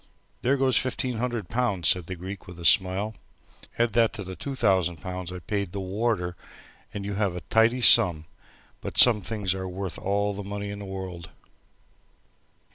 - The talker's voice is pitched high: No, low, 100 Hz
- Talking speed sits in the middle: Yes, average, 180 wpm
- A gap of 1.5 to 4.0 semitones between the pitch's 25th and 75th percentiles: Yes, average, 3.5 semitones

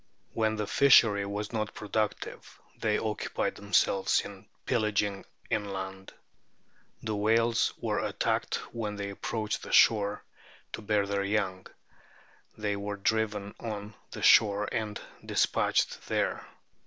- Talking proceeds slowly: Yes, slow, 125 wpm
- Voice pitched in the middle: No, low, 105 Hz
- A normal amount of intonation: No, narrow, 1.3 semitones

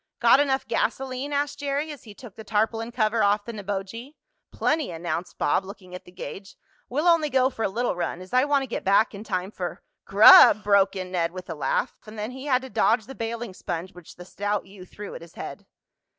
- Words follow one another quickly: Yes, fast, 230 wpm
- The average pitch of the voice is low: No, high, 215 Hz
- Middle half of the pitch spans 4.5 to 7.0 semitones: Yes, average, 5.3 semitones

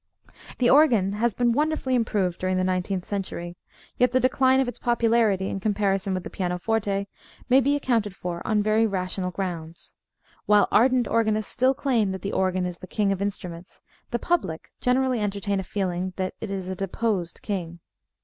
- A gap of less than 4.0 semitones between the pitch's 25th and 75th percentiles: No, average, 4.3 semitones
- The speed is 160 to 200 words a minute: Yes, average, 180 wpm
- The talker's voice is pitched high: Yes, high, 200 Hz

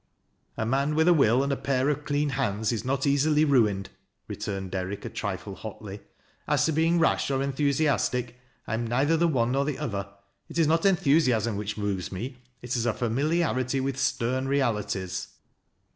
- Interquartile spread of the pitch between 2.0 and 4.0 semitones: No, average, 4.6 semitones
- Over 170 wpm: Yes, average, 180 wpm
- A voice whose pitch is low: Yes, low, 130 Hz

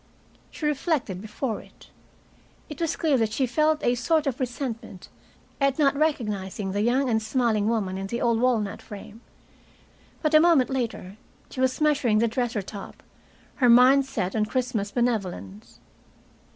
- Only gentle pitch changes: No, average, 4.5 semitones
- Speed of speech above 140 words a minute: Yes, average, 155 wpm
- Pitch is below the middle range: No, high, 240 Hz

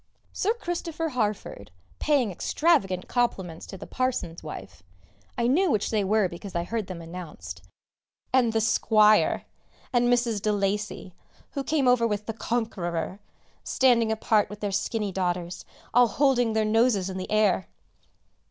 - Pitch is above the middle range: Yes, high, 215 Hz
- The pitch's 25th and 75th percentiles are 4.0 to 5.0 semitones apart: Yes, average, 4.5 semitones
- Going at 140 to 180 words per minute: Yes, average, 150 wpm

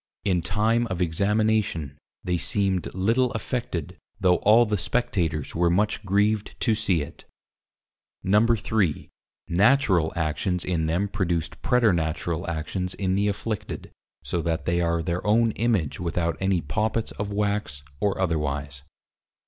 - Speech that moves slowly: Yes, slow, 130 wpm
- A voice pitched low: Yes, very low, 95 Hz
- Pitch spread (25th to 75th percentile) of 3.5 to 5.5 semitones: Yes, average, 4.1 semitones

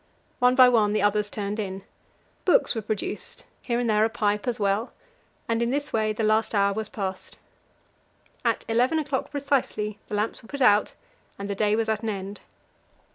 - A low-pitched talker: No, high, 215 Hz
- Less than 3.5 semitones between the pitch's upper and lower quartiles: Yes, narrow, 2.5 semitones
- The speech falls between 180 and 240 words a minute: Yes, average, 190 wpm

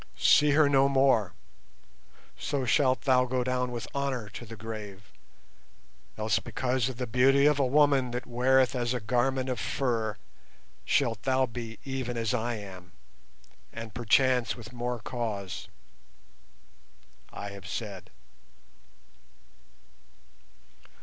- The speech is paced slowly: Yes, slow, 125 wpm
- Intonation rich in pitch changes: No, average, 2.9 semitones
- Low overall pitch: Yes, low, 125 Hz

